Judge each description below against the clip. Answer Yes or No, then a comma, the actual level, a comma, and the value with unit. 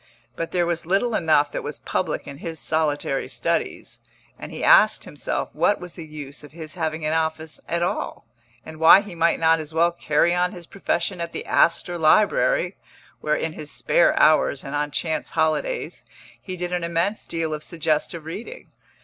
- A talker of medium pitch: Yes, medium, 165 Hz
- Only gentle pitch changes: Yes, narrow, 2.2 semitones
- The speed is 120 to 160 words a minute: No, average, 185 wpm